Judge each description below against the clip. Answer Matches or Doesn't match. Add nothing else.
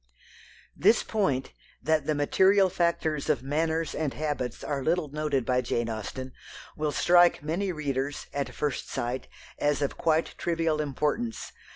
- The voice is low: Doesn't match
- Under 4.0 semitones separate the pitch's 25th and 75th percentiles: Matches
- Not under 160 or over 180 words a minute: Doesn't match